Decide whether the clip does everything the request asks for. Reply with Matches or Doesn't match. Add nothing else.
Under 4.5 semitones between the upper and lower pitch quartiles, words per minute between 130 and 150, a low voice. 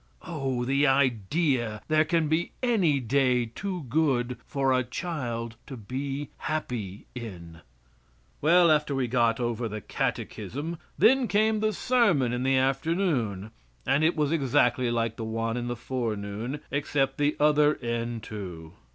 Doesn't match